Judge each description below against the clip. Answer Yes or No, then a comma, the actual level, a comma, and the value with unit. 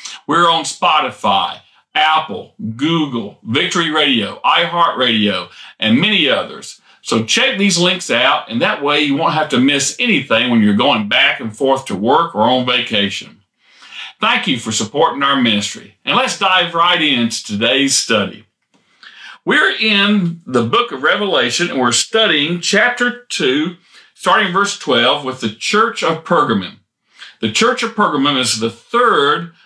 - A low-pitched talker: No, medium, 160 Hz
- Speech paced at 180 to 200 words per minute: No, average, 155 wpm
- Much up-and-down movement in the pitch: Yes, wide, 7.9 semitones